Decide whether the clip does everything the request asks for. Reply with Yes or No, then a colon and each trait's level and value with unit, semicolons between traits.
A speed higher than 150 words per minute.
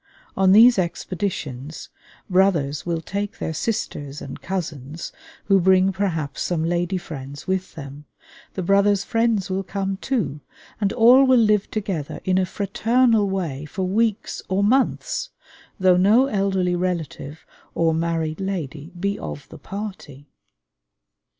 No: slow, 135 wpm